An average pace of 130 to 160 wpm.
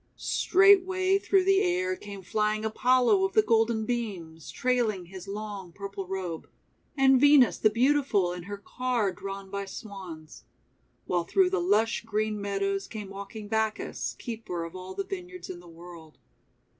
Yes: average, 155 wpm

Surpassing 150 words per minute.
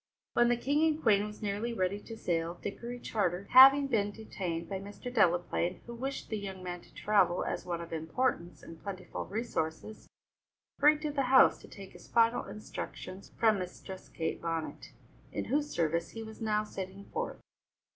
Yes: average, 175 wpm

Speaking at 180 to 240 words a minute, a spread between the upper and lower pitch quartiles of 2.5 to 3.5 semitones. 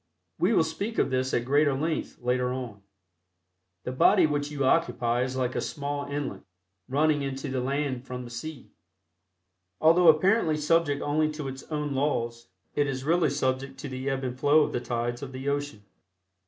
Yes: average, 185 wpm; average, 2.8 semitones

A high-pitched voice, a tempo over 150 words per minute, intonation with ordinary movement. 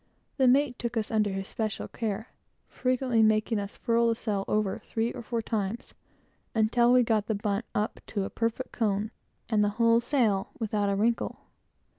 No: high, 220 Hz; average, 180 wpm; narrow, 2.3 semitones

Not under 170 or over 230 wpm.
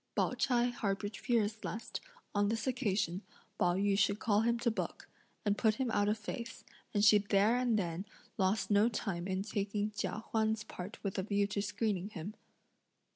Yes: average, 180 wpm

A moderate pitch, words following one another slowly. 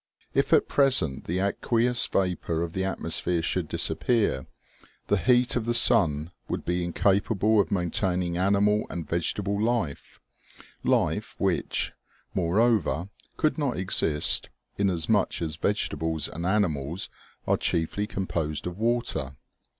No: very low, 95 Hz; slow, 125 wpm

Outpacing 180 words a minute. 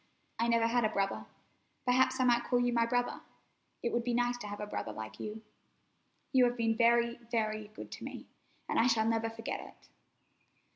Yes: average, 200 wpm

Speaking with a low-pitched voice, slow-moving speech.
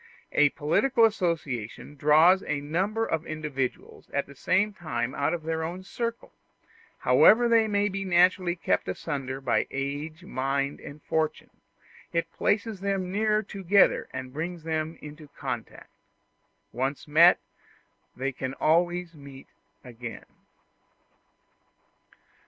No: medium, 160 Hz; slow, 125 wpm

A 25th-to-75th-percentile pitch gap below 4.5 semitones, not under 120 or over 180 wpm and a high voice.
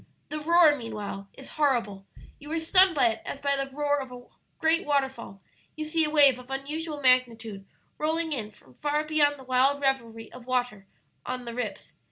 No: average, 4.1 semitones; average, 190 wpm; very high, 270 Hz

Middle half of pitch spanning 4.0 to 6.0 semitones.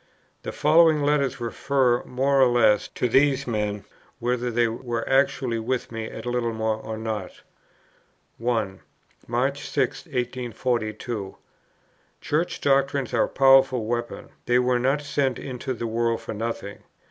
No: average, 2.8 semitones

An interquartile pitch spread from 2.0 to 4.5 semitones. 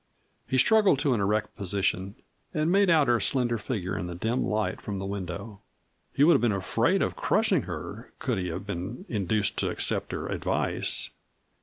No: average, 5.0 semitones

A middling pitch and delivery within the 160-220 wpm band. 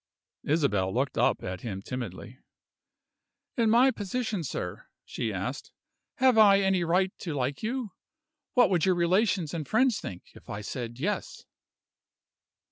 No: medium, 175 Hz; average, 140 wpm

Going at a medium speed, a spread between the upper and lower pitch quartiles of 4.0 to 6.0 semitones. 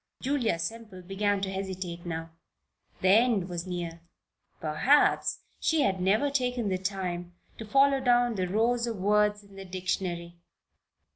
Yes: average, 145 wpm; average, 4.4 semitones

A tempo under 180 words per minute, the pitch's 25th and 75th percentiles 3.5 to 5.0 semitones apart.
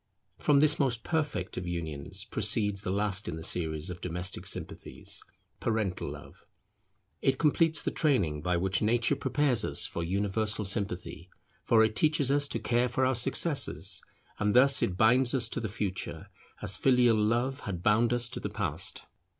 No: average, 170 wpm; wide, 5.5 semitones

